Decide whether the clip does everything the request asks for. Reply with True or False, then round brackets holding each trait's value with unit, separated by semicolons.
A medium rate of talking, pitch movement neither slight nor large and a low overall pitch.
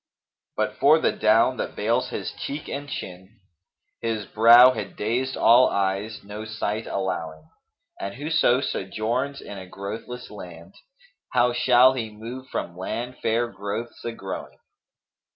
True (150 wpm; 3.9 semitones; 110 Hz)